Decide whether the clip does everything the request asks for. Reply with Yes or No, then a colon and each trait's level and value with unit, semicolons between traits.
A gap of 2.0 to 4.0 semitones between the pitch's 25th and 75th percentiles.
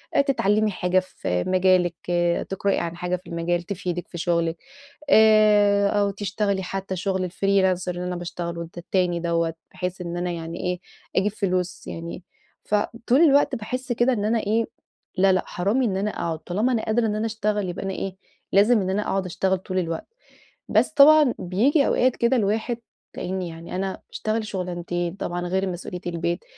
Yes: average, 3.2 semitones